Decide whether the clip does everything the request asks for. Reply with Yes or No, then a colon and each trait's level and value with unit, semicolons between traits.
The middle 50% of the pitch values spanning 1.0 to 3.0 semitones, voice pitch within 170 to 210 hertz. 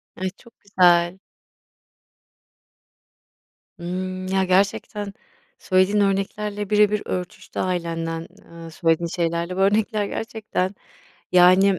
Yes: narrow, 2.6 semitones; medium, 185 Hz